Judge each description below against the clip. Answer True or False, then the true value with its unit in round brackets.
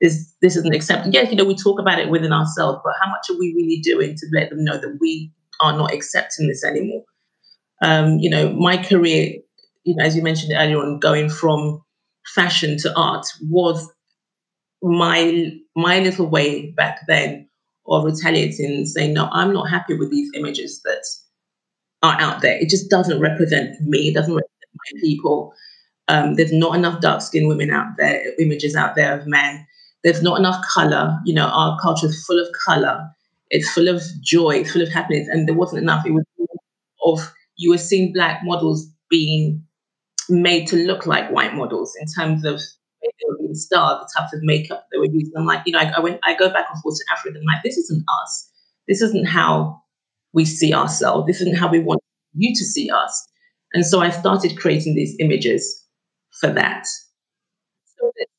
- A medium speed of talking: True (195 wpm)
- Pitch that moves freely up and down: False (3.2 semitones)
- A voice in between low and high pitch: True (170 Hz)